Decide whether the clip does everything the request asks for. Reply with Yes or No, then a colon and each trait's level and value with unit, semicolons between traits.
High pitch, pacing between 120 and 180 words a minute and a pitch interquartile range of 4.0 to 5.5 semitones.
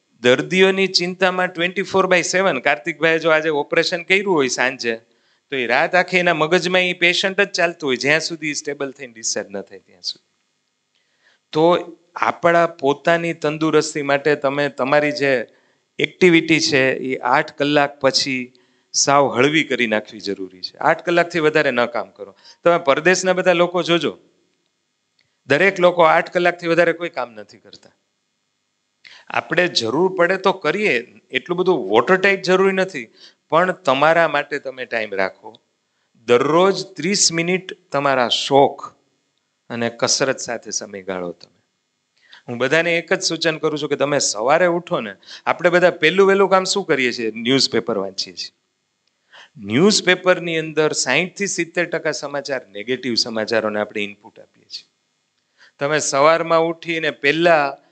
No: medium, 155 Hz; fast, 140 wpm; average, 5.1 semitones